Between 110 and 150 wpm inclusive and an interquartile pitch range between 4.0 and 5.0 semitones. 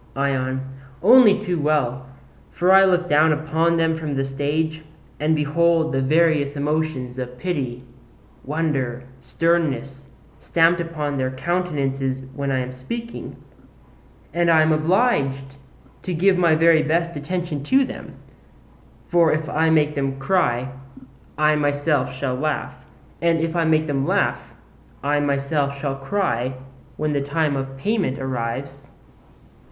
No: slow, 135 wpm; average, 3.5 semitones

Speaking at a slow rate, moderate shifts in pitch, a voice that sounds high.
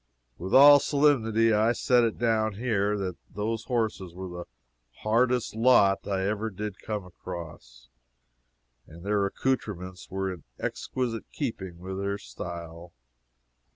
No: slow, 130 wpm; average, 3.7 semitones; low, 105 Hz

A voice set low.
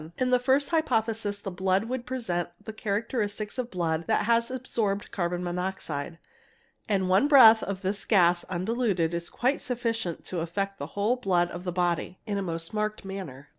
No: high, 200 Hz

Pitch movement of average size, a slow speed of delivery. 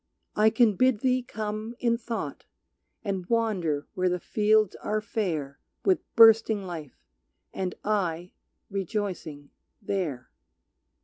Yes: average, 4.0 semitones; slow, 115 wpm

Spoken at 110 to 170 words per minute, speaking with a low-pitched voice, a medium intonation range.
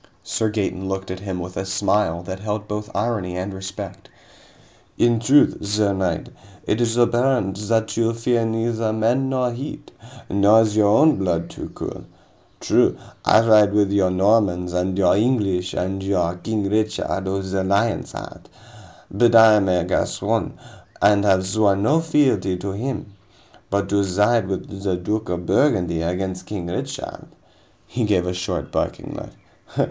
Yes: average, 165 wpm; low, 100 Hz; average, 3.1 semitones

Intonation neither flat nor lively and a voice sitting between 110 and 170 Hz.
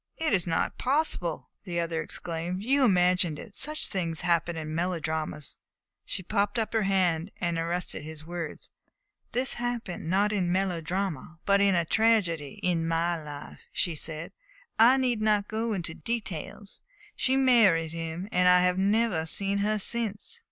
No: average, 4.4 semitones; medium, 180 Hz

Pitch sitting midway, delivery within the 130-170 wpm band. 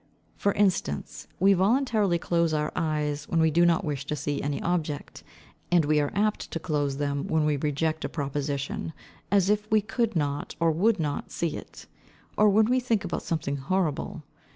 No: medium, 160 Hz; average, 185 wpm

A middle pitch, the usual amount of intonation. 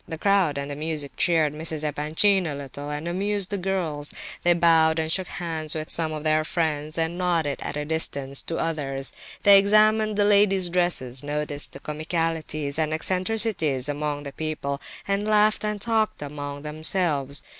Yes: medium, 160 Hz; average, 4.0 semitones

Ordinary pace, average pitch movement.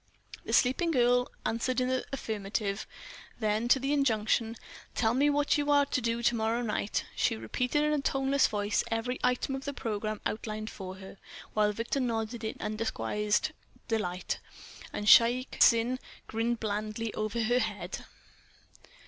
Yes: average, 155 wpm; average, 3.0 semitones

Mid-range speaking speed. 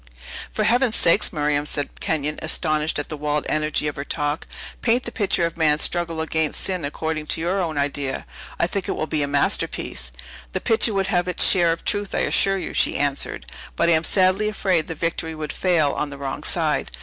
No: fast, 210 wpm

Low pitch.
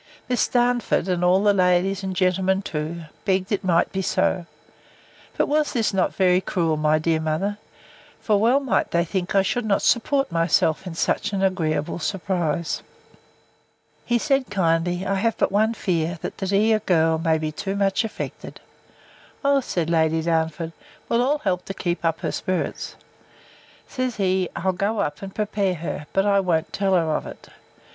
No: medium, 185 Hz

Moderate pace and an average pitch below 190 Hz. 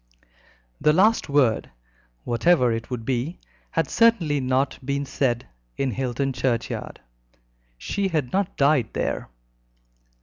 No: slow, 115 wpm; low, 135 Hz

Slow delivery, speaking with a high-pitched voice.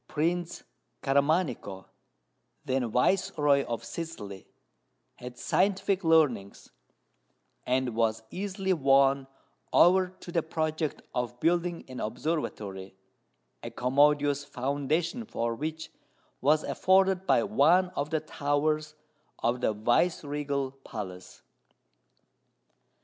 No: slow, 95 wpm; medium, 145 Hz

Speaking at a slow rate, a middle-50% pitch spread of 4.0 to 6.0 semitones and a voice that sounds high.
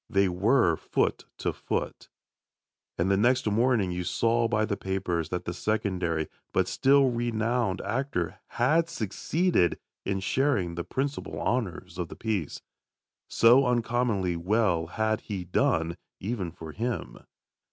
No: slow, 130 wpm; average, 5.2 semitones; low, 105 Hz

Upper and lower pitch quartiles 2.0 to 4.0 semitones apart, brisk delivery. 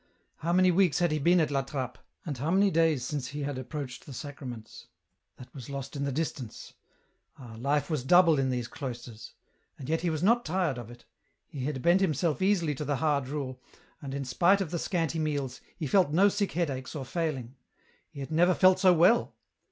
No: average, 4.5 semitones; fast, 210 wpm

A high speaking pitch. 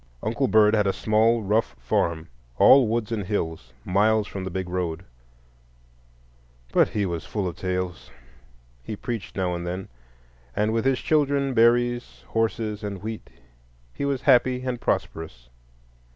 No: low, 100 Hz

